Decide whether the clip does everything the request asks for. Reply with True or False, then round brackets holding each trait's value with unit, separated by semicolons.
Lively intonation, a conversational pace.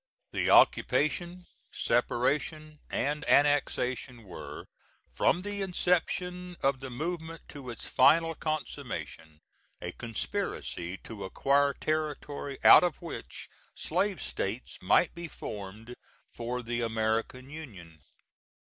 False (5.8 semitones; 105 wpm)